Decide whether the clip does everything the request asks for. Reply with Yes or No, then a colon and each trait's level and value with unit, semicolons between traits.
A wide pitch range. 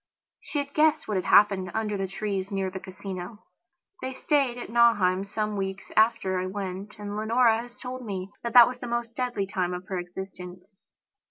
No: average, 3.8 semitones